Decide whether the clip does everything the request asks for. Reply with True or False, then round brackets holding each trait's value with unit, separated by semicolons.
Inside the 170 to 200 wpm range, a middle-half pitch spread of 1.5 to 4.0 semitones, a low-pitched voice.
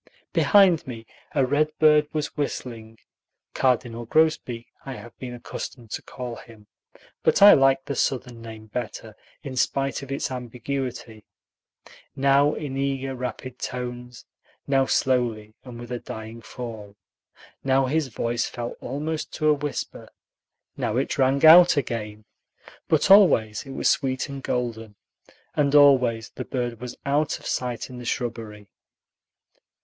False (140 wpm; 3.1 semitones; 125 Hz)